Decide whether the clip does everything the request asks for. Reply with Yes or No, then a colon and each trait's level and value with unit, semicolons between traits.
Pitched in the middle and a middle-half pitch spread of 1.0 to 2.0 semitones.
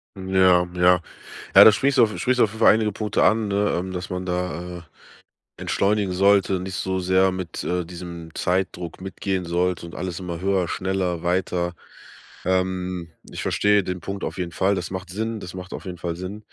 No: very low, 95 Hz; narrow, 1.7 semitones